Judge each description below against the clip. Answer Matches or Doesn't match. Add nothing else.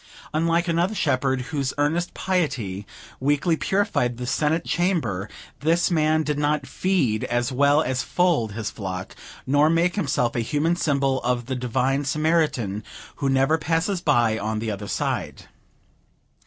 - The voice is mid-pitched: Matches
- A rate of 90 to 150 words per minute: Matches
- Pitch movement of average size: Matches